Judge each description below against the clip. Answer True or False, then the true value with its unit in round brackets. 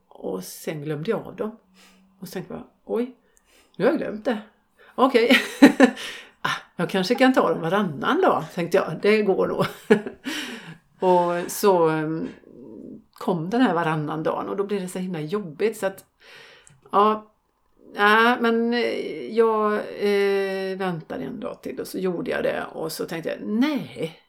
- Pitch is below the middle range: False (205 Hz)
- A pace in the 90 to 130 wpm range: False (160 wpm)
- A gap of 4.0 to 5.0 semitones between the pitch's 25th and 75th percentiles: True (4.4 semitones)